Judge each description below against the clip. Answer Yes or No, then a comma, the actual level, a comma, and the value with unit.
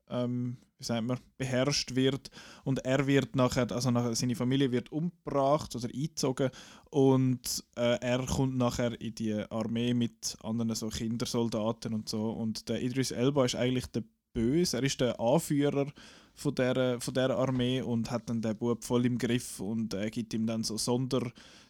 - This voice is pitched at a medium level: No, low, 125 Hz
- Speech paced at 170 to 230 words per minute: Yes, average, 180 wpm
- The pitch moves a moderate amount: No, narrow, 2.3 semitones